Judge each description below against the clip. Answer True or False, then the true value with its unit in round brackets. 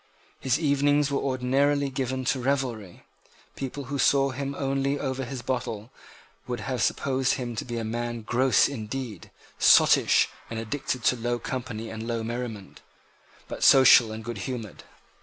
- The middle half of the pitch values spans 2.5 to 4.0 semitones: True (2.8 semitones)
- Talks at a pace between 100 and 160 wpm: True (150 wpm)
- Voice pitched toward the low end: True (125 Hz)